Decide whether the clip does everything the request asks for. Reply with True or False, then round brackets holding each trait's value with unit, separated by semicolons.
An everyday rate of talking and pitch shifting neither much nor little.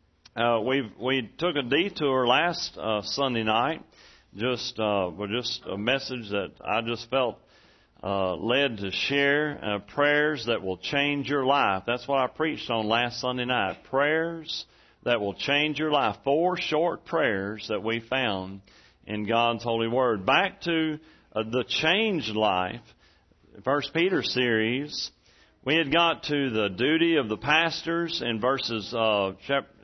True (155 wpm; 5.0 semitones)